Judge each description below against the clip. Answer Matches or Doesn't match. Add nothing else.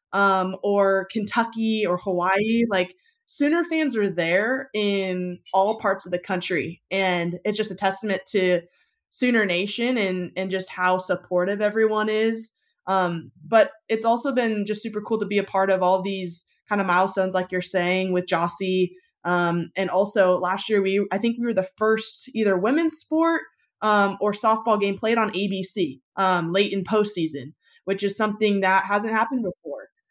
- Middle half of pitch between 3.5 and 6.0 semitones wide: Doesn't match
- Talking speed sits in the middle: Matches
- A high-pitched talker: Matches